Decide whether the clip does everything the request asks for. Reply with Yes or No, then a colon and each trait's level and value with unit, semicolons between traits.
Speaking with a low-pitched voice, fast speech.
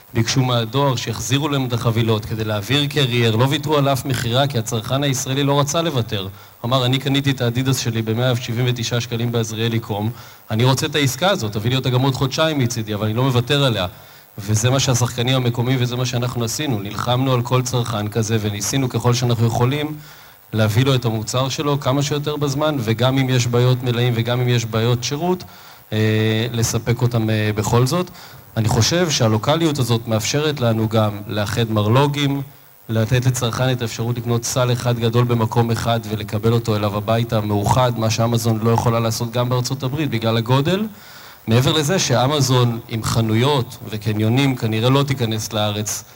Yes: low, 120 Hz; fast, 170 wpm